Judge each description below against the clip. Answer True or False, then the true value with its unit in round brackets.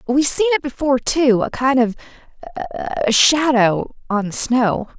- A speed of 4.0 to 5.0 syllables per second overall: True (4.5 syllables/s)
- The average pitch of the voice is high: True (255 Hz)